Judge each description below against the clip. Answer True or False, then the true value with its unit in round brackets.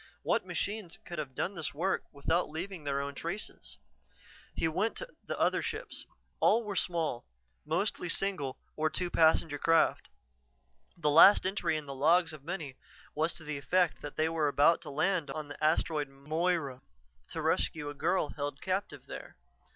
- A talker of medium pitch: True (160 Hz)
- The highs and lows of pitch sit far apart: False (3.6 semitones)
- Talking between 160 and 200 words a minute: True (170 wpm)